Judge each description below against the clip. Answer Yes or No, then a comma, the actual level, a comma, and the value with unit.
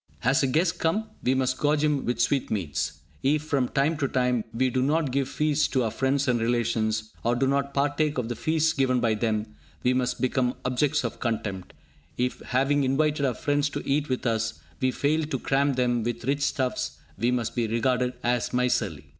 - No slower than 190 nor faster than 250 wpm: Yes, average, 200 wpm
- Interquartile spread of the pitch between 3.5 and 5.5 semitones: No, average, 3.0 semitones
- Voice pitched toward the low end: Yes, low, 130 Hz